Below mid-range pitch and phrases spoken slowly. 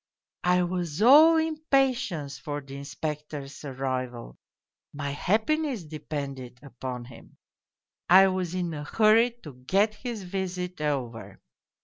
No: medium, 160 Hz; slow, 115 wpm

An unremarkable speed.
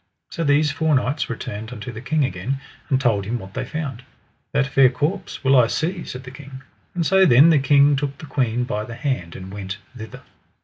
No: fast, 215 wpm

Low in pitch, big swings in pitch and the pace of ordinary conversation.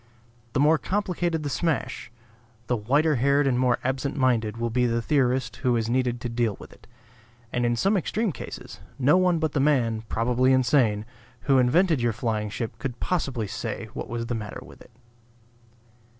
No: low, 125 Hz; average, 3.8 semitones; average, 180 wpm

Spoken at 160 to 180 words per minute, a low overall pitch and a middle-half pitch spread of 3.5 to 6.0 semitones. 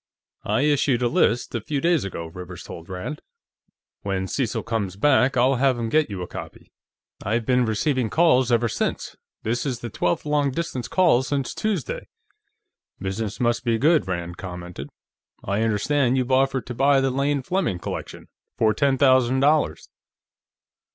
Yes: average, 165 wpm; low, 125 Hz; average, 4.9 semitones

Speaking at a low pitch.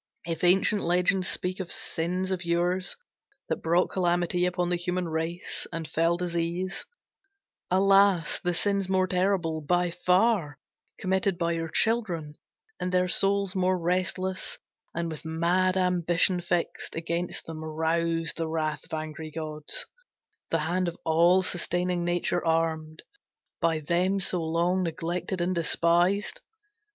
No: medium, 175 Hz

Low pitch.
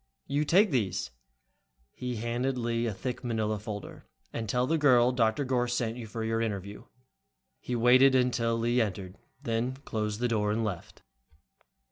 Yes: low, 115 Hz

